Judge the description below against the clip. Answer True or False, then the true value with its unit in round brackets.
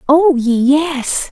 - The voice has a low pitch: False (285 Hz)